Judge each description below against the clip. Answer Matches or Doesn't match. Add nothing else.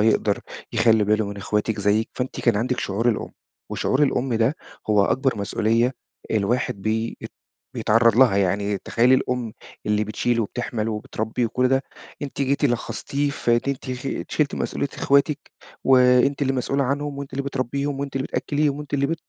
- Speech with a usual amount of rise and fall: Matches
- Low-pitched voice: Matches